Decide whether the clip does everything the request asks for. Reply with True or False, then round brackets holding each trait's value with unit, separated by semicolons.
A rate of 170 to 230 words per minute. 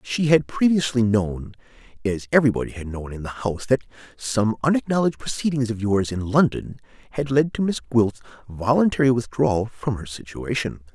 False (160 wpm)